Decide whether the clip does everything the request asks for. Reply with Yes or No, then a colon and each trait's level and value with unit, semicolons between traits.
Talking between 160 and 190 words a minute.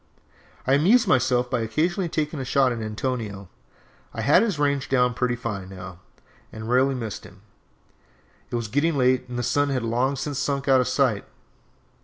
Yes: average, 180 wpm